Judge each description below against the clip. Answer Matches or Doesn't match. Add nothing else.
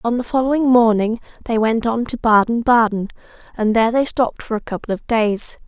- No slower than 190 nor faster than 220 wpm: Matches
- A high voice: Matches